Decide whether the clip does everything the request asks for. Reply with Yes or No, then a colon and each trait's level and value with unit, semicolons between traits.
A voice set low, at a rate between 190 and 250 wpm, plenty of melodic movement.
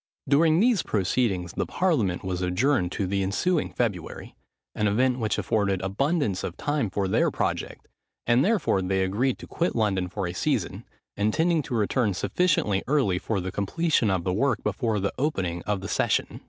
No: low, 105 Hz; average, 175 wpm; wide, 6.6 semitones